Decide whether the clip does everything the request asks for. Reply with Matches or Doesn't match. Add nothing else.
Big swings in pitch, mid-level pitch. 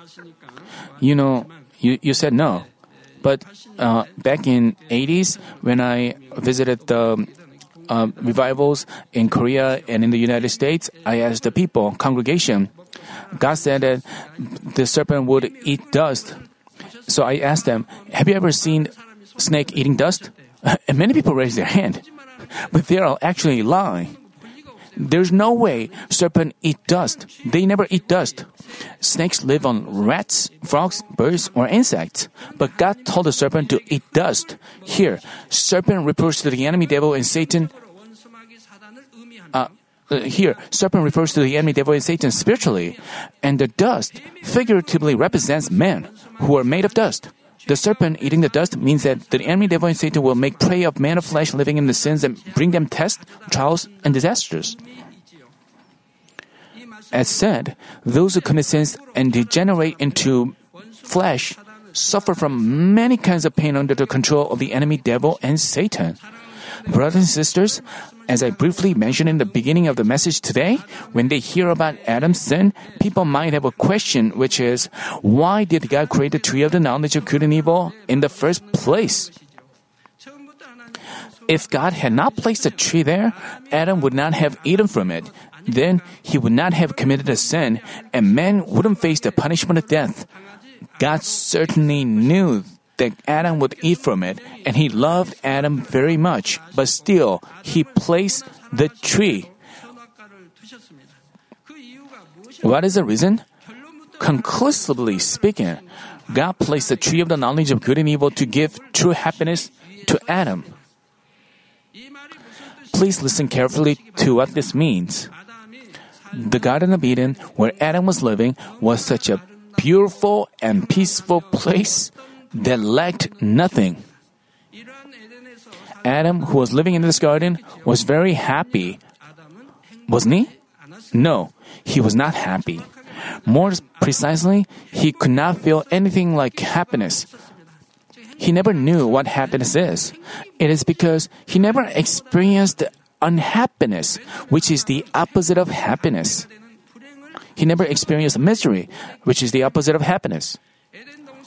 Matches